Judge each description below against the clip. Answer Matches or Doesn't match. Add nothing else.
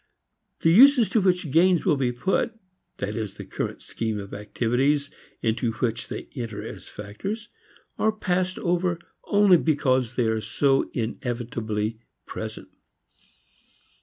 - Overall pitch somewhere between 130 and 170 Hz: Matches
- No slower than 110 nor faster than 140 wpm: Matches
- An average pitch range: Doesn't match